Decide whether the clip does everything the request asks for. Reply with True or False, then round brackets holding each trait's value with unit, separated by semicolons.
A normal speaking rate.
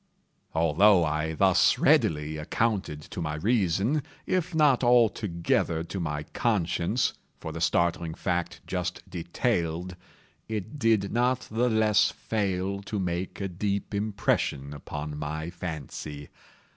False (120 wpm)